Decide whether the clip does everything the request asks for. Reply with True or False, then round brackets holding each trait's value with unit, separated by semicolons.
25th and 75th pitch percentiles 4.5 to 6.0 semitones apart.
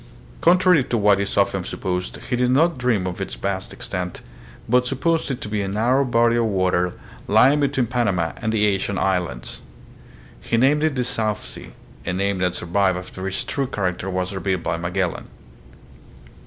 True (5.3 semitones)